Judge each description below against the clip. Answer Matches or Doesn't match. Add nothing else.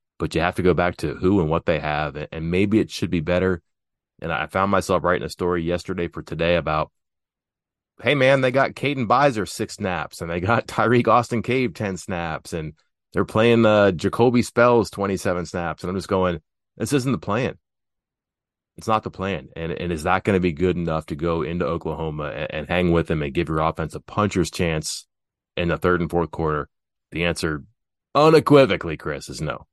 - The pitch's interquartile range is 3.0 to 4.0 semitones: Doesn't match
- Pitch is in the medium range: Doesn't match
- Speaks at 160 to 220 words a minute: Matches